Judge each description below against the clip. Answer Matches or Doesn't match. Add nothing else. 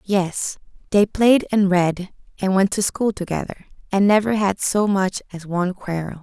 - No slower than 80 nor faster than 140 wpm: Doesn't match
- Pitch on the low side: Doesn't match